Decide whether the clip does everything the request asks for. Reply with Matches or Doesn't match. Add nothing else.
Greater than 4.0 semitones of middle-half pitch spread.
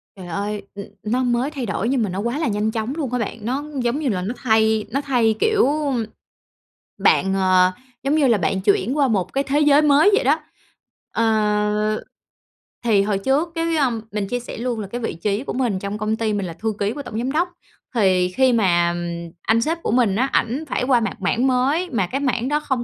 Matches